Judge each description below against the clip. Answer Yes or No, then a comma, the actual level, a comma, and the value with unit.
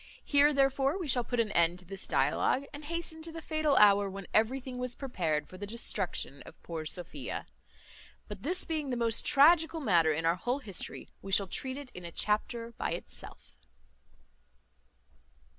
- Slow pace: No, average, 175 wpm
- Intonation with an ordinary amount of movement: No, wide, 7.1 semitones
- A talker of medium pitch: No, high, 235 Hz